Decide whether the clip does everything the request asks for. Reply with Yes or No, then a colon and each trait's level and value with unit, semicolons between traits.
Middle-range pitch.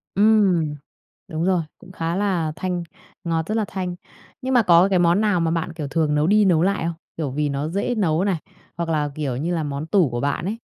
Yes: medium, 170 Hz